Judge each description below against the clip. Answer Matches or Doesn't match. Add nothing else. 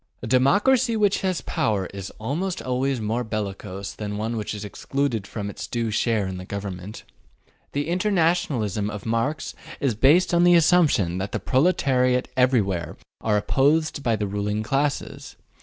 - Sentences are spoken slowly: Doesn't match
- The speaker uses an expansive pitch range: Matches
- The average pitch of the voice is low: Matches